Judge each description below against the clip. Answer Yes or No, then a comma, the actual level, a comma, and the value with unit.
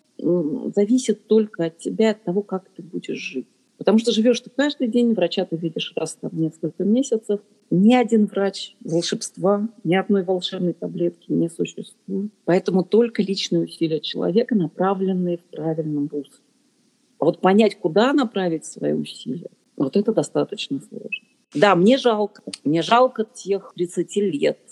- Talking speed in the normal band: Yes, average, 150 wpm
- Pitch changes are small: No, average, 4.2 semitones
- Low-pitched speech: No, high, 200 Hz